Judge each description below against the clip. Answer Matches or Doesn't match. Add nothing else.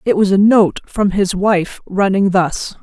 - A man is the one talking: Doesn't match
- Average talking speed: Matches